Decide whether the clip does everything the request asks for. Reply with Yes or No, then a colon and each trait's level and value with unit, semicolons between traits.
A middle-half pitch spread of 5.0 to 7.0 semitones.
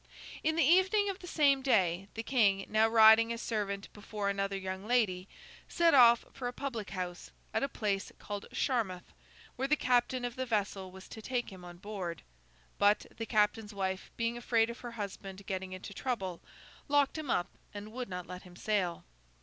No: average, 4.3 semitones